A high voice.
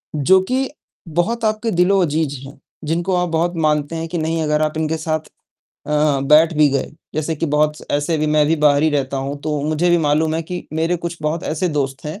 No: medium, 155 Hz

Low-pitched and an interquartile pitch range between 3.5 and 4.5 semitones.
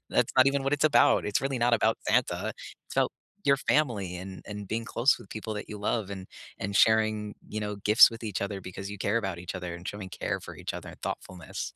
No: low, 105 Hz; average, 3.1 semitones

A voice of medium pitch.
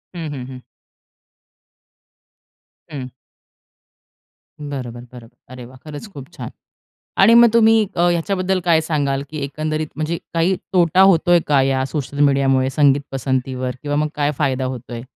Yes: medium, 145 Hz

